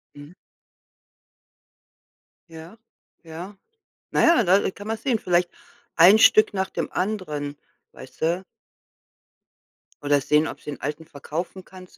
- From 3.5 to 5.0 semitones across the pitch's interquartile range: Yes, average, 4.3 semitones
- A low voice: No, medium, 175 Hz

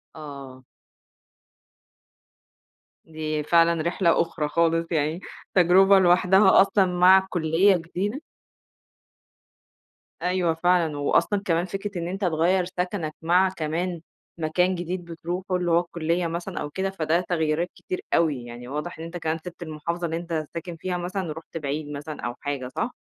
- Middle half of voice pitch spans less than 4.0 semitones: Yes, narrow, 2.5 semitones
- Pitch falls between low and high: Yes, medium, 170 Hz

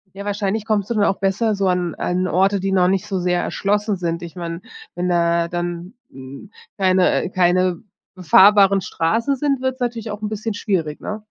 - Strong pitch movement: No, average, 2.9 semitones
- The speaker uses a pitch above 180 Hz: Yes, high, 190 Hz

